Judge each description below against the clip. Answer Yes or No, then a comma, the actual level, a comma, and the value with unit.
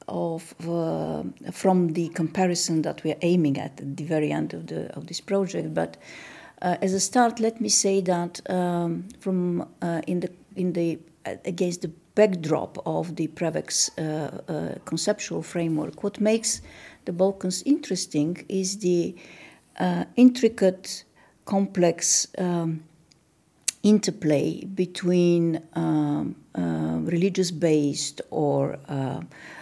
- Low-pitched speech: No, medium, 170 Hz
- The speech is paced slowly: Yes, slow, 130 wpm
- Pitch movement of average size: Yes, average, 3.3 semitones